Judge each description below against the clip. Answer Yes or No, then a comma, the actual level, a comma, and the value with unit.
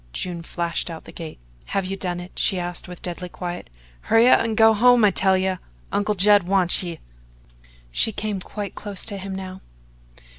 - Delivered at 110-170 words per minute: No, average, 190 wpm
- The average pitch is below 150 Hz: No, high, 190 Hz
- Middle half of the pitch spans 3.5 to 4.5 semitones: No, average, 2.7 semitones